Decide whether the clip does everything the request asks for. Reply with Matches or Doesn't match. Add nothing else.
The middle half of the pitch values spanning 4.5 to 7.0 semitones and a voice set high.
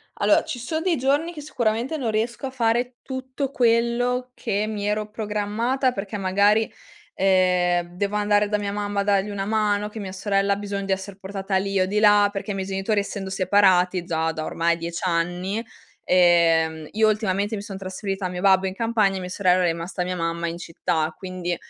Doesn't match